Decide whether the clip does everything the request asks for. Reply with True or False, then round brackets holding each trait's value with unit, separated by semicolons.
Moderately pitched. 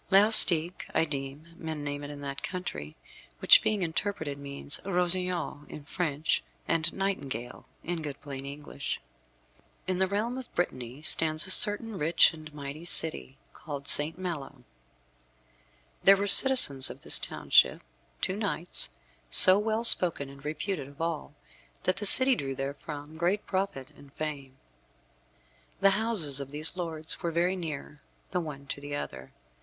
True (160 Hz)